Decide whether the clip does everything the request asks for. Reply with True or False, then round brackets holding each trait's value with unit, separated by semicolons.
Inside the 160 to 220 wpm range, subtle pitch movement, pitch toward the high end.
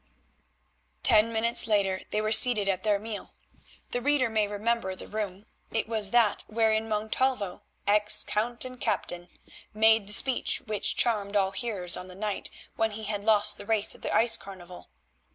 True (170 wpm; 2.0 semitones; 215 Hz)